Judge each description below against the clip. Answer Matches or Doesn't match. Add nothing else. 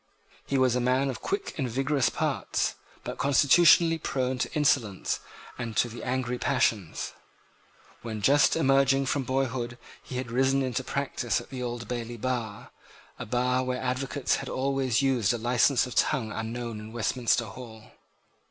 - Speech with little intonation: Matches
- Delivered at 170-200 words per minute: Doesn't match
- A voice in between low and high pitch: Doesn't match